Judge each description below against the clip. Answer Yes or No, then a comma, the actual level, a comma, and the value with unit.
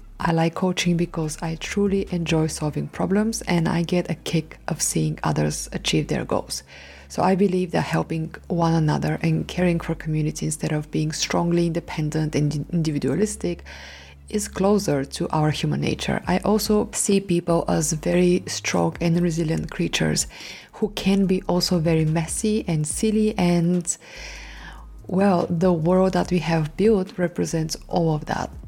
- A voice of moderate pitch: Yes, medium, 170 Hz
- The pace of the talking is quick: No, average, 155 wpm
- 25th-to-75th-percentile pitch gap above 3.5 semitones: No, average, 3.2 semitones